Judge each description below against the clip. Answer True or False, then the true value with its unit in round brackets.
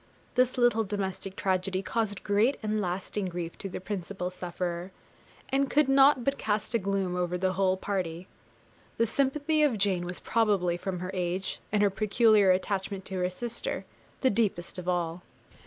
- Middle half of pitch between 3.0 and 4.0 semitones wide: True (3.7 semitones)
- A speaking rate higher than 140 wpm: True (170 wpm)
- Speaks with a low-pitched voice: False (195 Hz)